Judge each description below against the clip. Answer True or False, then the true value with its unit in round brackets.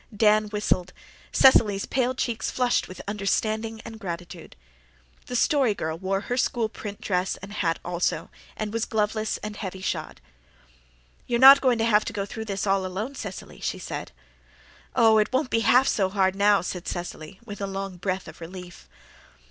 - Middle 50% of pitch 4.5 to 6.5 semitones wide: False (3.1 semitones)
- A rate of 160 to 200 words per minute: True (175 wpm)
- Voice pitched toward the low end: False (205 Hz)